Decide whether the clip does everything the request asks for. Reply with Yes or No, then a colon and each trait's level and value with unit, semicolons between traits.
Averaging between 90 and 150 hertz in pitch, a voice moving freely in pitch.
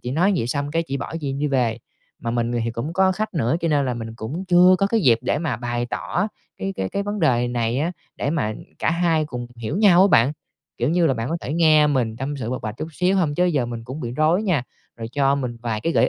Yes: medium, 140 Hz; wide, 5.7 semitones